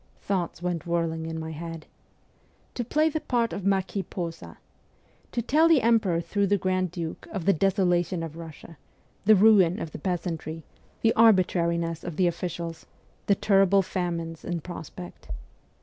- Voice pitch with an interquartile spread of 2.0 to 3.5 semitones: Yes, average, 3.1 semitones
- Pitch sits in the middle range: Yes, medium, 180 Hz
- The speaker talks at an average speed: Yes, average, 155 wpm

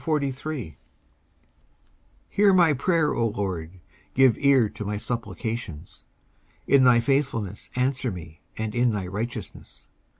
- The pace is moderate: No, slow, 120 wpm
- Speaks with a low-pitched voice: Yes, low, 120 Hz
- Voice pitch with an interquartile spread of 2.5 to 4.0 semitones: No, average, 5.1 semitones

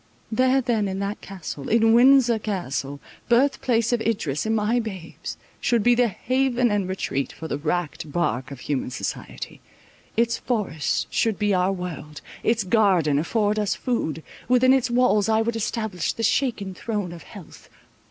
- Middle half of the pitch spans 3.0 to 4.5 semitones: No, average, 5.0 semitones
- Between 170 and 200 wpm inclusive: No, average, 160 wpm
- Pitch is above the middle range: Yes, high, 210 Hz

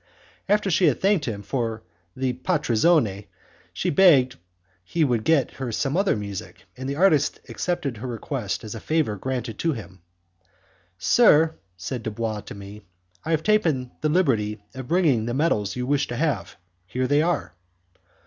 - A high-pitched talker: No, low, 130 Hz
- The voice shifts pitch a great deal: Yes, wide, 6.3 semitones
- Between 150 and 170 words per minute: Yes, average, 165 wpm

